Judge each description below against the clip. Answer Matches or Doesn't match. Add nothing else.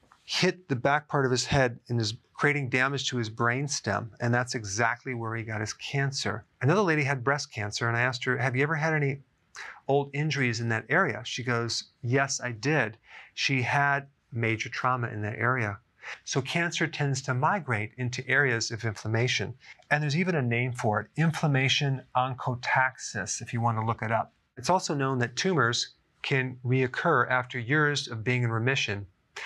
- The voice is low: Matches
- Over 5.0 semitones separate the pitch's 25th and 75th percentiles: Doesn't match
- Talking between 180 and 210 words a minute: Matches